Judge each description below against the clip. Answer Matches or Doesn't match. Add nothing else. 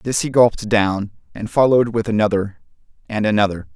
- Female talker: Doesn't match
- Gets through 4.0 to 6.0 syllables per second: Matches